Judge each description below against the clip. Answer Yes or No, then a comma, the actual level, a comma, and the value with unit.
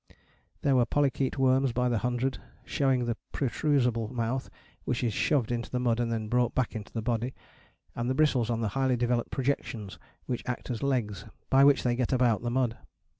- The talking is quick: No, average, 195 wpm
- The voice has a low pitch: Yes, low, 125 Hz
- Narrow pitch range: Yes, narrow, 2.1 semitones